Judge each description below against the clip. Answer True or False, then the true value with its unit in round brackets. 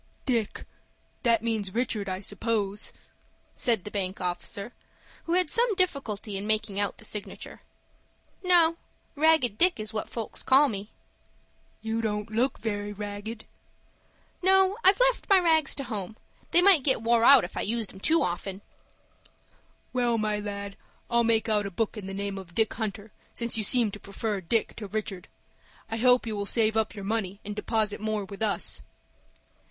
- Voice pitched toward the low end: False (220 Hz)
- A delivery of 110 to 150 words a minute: False (170 wpm)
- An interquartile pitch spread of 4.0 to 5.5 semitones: False (3.2 semitones)